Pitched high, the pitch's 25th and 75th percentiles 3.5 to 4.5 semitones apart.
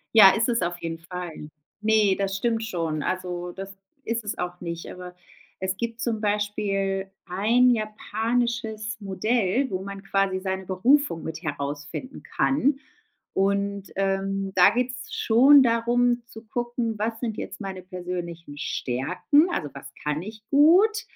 Yes: high, 200 Hz; average, 4.2 semitones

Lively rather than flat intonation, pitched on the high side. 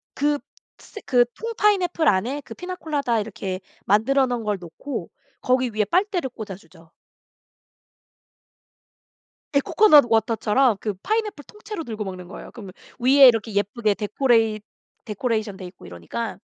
Yes: wide, 5.7 semitones; high, 235 Hz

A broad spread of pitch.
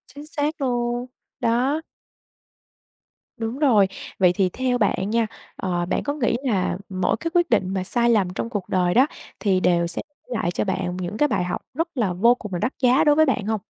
Yes: wide, 5.7 semitones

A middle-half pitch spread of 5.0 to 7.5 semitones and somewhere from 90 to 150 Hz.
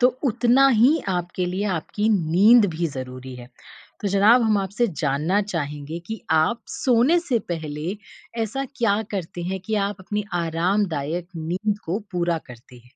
No: wide, 5.4 semitones; medium, 185 Hz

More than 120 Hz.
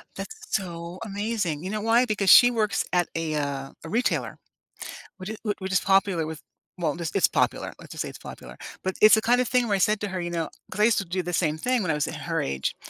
Yes: high, 190 Hz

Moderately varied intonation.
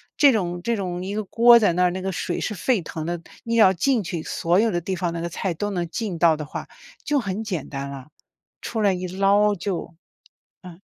Yes: average, 3.4 semitones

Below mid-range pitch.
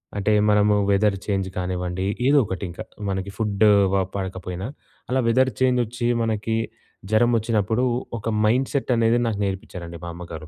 Yes: low, 105 Hz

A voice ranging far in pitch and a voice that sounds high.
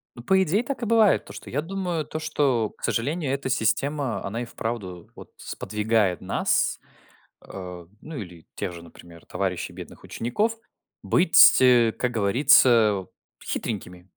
No: wide, 7.6 semitones; low, 120 Hz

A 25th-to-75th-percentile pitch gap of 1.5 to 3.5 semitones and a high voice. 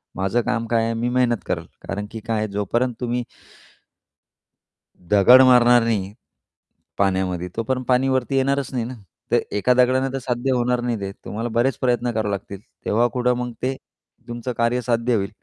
No: narrow, 2.5 semitones; low, 120 Hz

